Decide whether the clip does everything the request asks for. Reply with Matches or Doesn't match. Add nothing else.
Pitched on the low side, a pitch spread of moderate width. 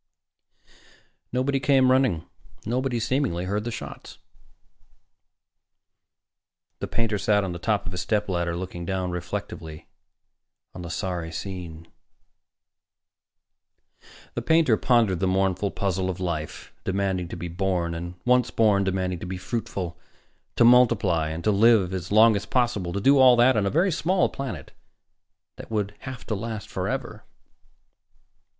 Matches